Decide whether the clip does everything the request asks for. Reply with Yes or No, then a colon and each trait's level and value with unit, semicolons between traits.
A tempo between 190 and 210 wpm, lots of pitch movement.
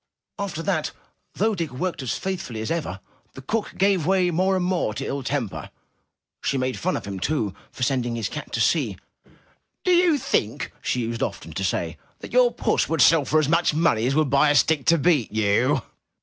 Yes: fast, 205 wpm; wide, 6.6 semitones